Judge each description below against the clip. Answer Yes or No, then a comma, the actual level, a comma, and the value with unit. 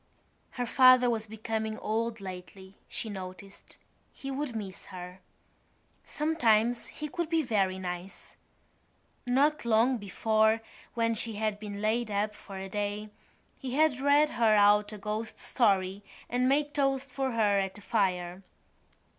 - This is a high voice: Yes, high, 220 Hz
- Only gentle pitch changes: No, average, 3.9 semitones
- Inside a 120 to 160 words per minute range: Yes, average, 145 wpm